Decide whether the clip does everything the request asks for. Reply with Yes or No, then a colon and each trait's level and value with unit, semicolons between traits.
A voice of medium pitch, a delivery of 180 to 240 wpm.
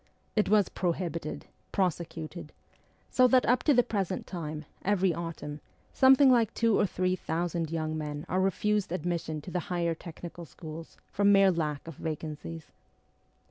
No: medium, 175 Hz; average, 150 wpm